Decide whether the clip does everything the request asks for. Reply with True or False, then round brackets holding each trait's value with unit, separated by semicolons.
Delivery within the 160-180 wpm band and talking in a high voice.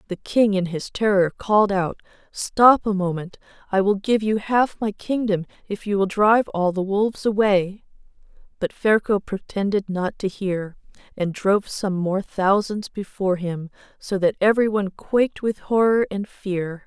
True (165 wpm; 200 Hz)